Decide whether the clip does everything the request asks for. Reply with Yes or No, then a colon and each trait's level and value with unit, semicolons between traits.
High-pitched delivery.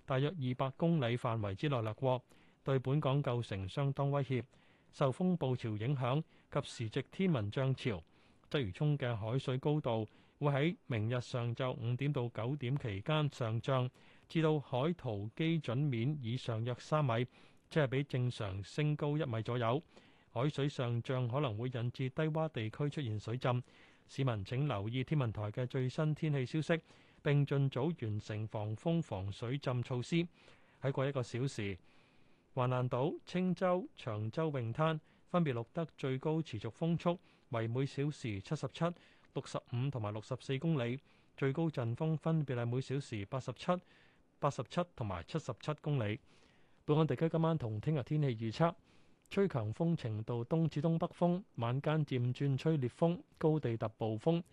No: low, 135 Hz